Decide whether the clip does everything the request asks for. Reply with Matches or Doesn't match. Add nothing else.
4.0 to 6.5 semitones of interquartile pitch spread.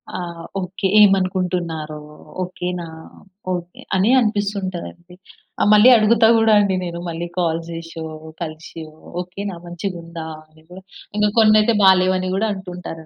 Doesn't match